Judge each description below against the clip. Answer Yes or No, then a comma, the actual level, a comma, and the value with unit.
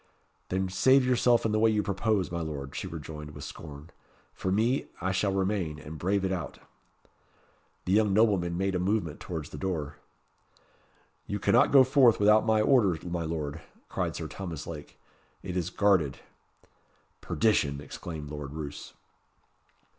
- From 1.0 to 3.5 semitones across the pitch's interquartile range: No, average, 5.2 semitones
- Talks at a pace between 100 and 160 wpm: Yes, average, 155 wpm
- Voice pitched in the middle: No, very low, 95 Hz